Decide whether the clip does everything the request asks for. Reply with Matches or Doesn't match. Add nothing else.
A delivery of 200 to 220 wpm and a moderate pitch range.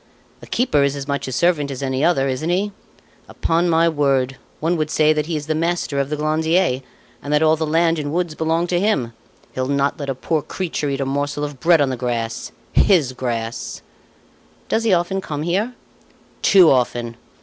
Matches